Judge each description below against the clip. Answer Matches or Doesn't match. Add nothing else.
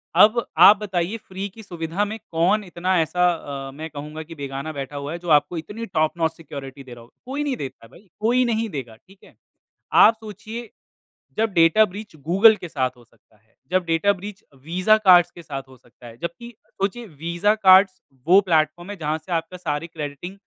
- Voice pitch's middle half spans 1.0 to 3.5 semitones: Doesn't match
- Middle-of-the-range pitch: Matches